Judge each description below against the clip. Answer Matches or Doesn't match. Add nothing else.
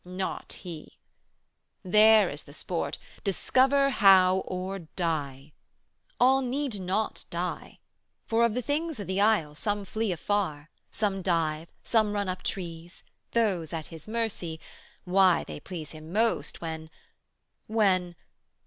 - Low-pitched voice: Doesn't match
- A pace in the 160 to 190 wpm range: Doesn't match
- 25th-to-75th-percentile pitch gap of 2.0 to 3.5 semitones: Doesn't match